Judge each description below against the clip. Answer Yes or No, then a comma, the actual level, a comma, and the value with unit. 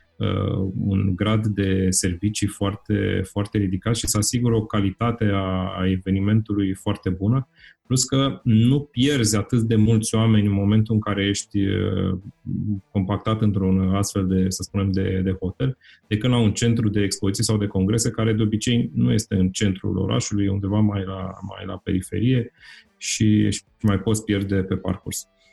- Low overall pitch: Yes, low, 100 Hz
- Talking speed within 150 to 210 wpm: Yes, average, 160 wpm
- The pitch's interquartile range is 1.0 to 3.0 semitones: Yes, narrow, 2.5 semitones